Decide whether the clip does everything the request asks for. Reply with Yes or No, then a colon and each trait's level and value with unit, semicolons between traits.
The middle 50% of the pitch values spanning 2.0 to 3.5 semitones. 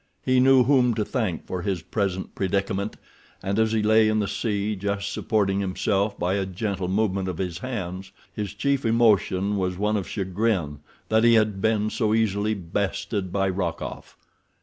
Yes: narrow, 2.6 semitones